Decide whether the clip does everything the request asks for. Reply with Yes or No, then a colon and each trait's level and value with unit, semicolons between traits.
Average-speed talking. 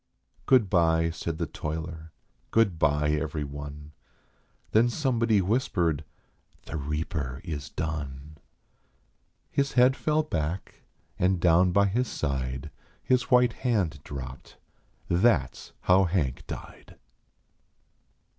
No: slow, 115 wpm